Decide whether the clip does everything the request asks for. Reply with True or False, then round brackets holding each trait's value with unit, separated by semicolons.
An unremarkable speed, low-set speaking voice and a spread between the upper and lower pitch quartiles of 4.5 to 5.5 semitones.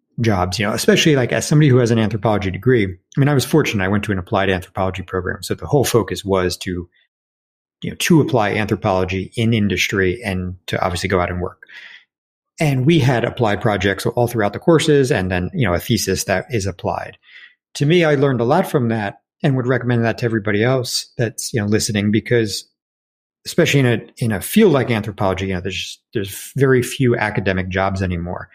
False (210 wpm; 110 Hz; 4.9 semitones)